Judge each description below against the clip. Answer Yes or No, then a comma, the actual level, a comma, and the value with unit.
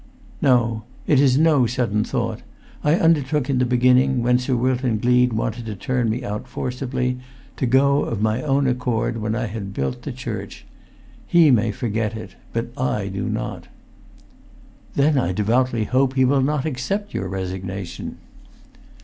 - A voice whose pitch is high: No, low, 125 Hz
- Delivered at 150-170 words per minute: Yes, average, 160 wpm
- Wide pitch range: No, average, 3.3 semitones